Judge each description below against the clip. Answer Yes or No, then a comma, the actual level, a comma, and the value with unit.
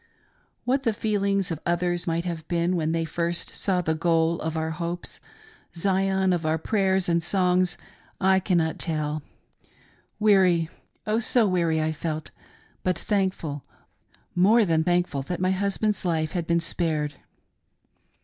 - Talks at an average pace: Yes, average, 160 wpm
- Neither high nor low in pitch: Yes, medium, 175 Hz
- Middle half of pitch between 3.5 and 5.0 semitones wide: No, average, 2.8 semitones